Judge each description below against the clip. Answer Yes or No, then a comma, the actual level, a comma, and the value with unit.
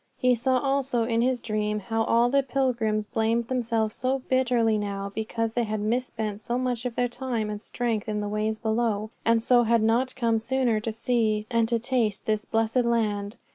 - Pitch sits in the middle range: No, high, 230 Hz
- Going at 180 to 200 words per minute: Yes, average, 195 wpm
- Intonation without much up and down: Yes, narrow, 2.2 semitones